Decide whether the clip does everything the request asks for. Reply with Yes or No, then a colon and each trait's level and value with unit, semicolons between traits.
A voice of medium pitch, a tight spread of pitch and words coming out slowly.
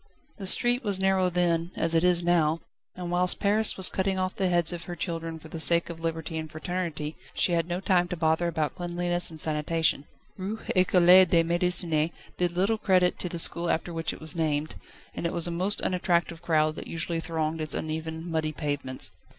No: medium, 170 Hz; narrow, 1.9 semitones; fast, 205 wpm